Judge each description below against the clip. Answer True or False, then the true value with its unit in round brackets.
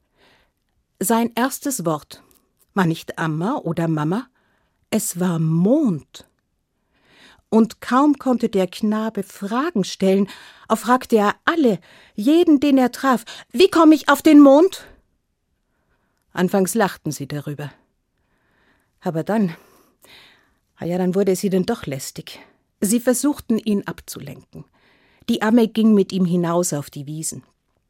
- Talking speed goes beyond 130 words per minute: False (125 wpm)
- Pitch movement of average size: False (6.3 semitones)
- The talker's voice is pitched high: True (205 Hz)